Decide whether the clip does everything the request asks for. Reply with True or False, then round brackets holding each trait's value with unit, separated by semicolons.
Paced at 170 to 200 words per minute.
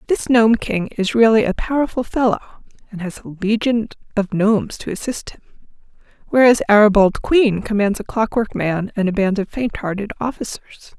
True (175 wpm)